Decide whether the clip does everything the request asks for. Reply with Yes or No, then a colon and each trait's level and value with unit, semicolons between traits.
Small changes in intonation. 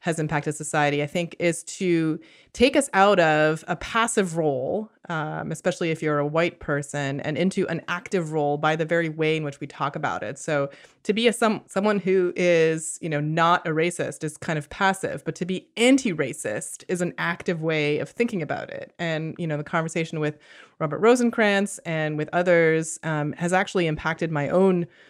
No: average, 3.2 semitones